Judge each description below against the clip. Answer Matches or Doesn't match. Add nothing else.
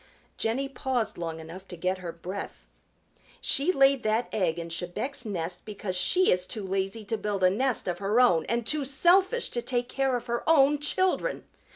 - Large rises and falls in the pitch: Matches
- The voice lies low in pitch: Doesn't match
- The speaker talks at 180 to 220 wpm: Matches